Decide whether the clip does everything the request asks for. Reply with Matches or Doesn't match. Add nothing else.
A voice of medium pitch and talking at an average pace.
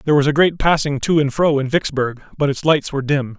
Doesn't match